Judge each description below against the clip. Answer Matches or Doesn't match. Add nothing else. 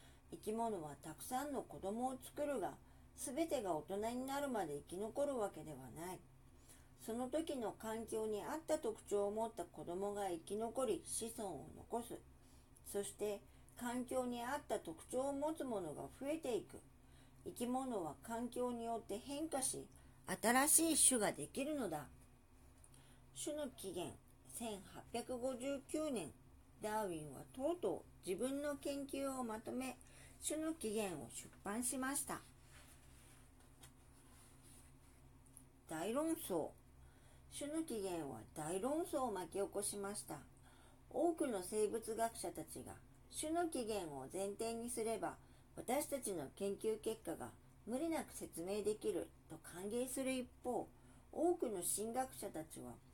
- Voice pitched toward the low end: Doesn't match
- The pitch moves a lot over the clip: Matches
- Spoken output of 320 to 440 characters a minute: Doesn't match